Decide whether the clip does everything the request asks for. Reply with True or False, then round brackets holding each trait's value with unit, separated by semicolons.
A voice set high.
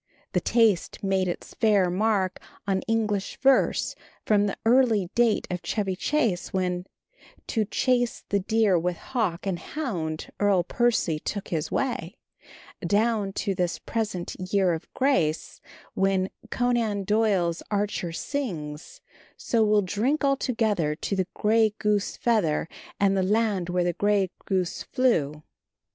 True (200 Hz)